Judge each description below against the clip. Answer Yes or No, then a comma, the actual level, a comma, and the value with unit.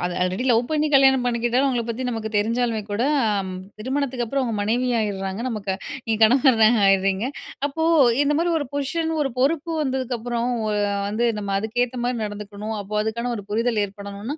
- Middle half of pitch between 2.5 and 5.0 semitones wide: Yes, average, 3.8 semitones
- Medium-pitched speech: No, high, 235 Hz